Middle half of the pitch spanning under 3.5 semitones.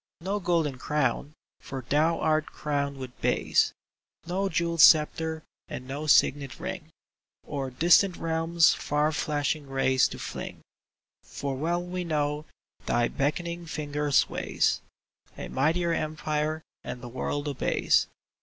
Yes: average, 2.8 semitones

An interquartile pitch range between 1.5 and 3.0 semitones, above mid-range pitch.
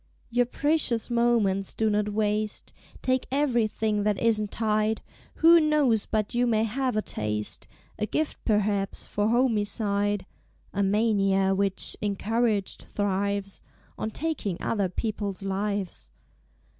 Yes: average, 2.7 semitones; high, 210 Hz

